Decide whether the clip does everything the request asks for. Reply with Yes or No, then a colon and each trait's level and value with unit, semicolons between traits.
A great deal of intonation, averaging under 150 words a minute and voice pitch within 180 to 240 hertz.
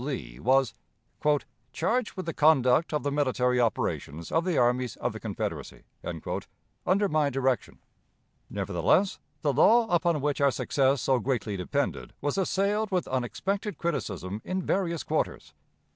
No: wide, 5.9 semitones; average, 140 wpm; medium, 145 Hz